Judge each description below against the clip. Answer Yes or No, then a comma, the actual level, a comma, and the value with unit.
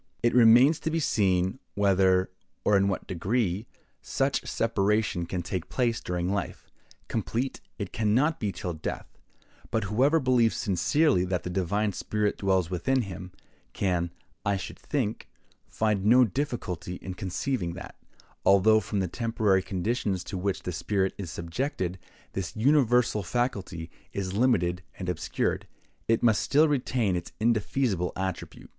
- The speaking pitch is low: Yes, low, 100 Hz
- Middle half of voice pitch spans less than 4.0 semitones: No, average, 4.4 semitones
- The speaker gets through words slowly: No, average, 145 wpm